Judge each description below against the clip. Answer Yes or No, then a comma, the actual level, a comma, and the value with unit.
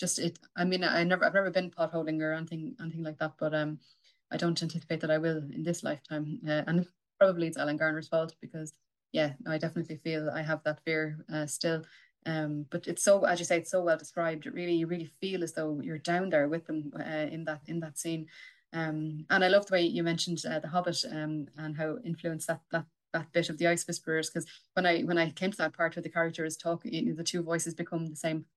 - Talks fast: Yes, fast, 250 wpm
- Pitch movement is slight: Yes, narrow, 1.5 semitones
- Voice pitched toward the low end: No, medium, 165 Hz